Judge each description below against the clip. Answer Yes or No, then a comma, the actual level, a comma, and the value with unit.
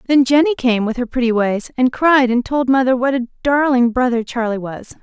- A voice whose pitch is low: No, very high, 250 Hz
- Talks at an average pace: No, fast, 215 wpm